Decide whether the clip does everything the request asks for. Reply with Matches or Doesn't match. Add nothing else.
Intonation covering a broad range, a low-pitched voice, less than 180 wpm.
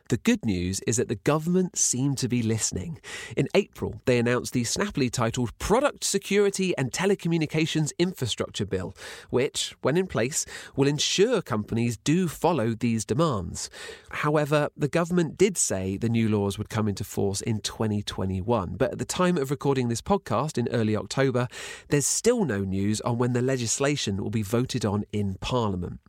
Matches